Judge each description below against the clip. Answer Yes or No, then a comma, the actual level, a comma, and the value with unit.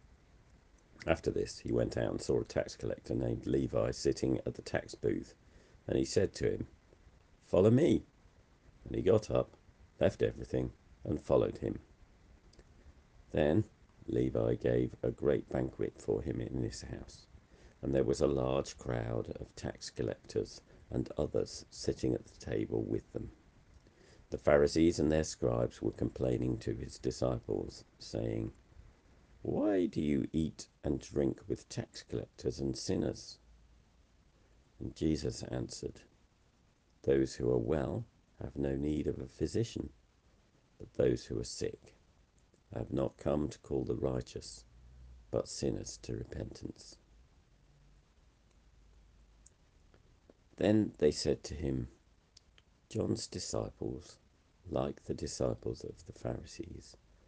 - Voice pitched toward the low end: Yes, very low, 75 Hz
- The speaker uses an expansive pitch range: No, average, 4.7 semitones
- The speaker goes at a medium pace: No, slow, 130 wpm